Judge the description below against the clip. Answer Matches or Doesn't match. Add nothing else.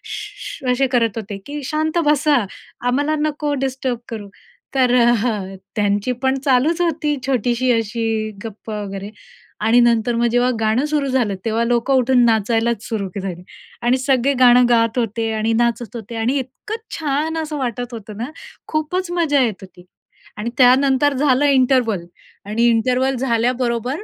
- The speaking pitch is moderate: Doesn't match